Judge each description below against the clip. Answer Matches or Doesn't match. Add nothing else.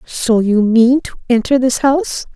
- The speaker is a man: Doesn't match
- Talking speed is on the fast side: Doesn't match